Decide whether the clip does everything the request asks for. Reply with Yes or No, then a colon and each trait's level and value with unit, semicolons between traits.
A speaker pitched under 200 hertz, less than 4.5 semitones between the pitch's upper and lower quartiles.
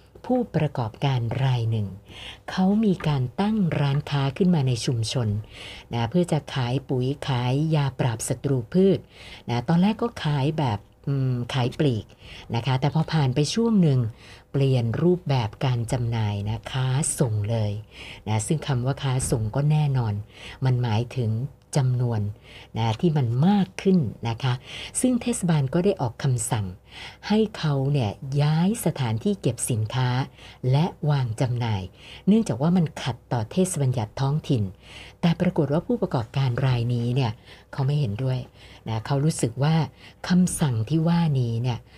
No: low, 135 Hz; average, 4.8 semitones